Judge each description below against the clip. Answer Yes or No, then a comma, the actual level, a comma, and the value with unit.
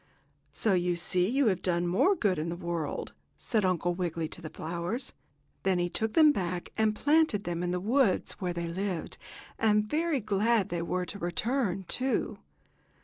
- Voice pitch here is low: No, medium, 185 Hz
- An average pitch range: Yes, average, 4.2 semitones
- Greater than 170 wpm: Yes, average, 180 wpm